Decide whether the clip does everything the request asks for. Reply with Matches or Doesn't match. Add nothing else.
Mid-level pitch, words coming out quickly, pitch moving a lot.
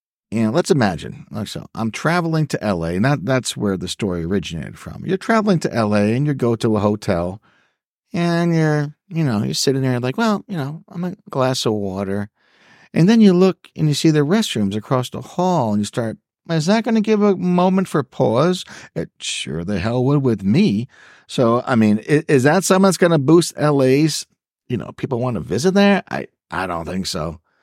Matches